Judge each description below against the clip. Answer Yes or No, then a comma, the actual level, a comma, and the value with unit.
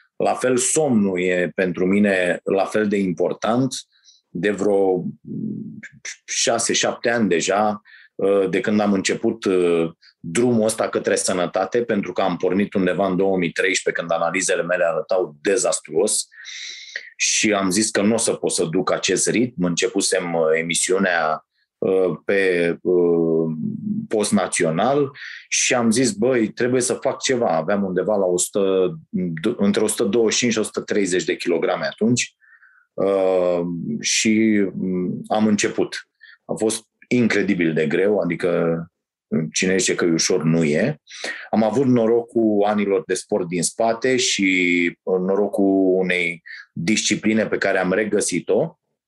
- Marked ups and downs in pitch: No, average, 3.5 semitones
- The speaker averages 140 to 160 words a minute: No, average, 130 wpm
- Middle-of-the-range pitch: No, very low, 95 Hz